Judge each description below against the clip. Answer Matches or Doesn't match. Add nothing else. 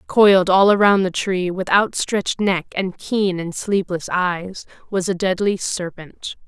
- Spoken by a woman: Matches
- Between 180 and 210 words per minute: Doesn't match